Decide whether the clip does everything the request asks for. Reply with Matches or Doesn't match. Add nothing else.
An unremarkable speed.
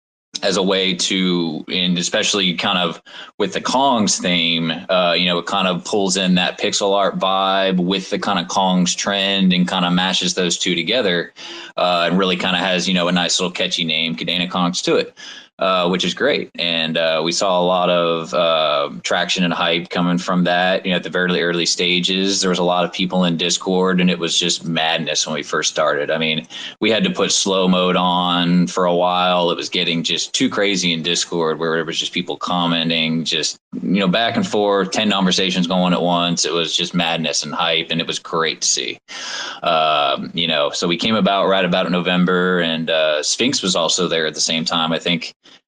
Doesn't match